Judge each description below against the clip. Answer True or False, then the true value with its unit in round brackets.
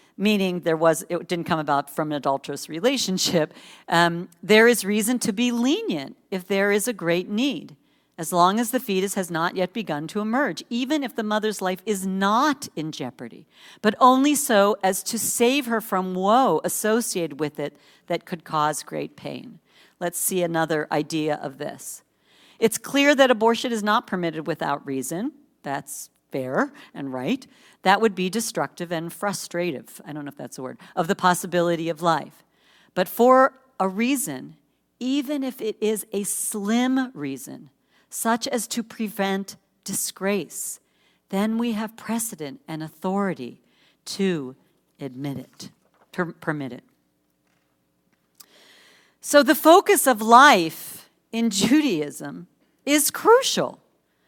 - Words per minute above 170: False (150 wpm)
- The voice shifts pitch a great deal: True (6.4 semitones)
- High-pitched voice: True (195 Hz)